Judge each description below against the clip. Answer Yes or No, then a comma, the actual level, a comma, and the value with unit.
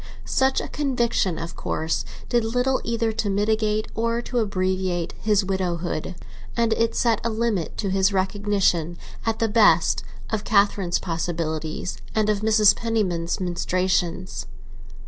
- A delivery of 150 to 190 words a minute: No, slow, 135 wpm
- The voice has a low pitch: No, high, 205 Hz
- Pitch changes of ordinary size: Yes, average, 3.7 semitones